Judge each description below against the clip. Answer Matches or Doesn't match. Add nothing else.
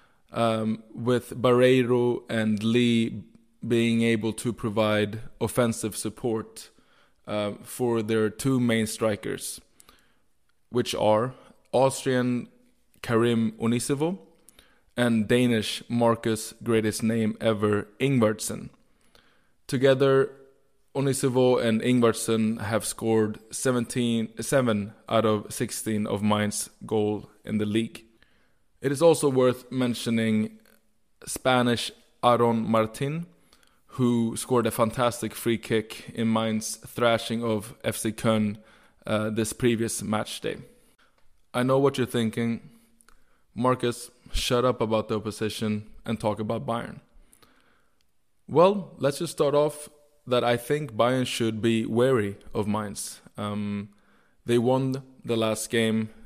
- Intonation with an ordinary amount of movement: Doesn't match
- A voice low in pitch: Matches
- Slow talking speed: Matches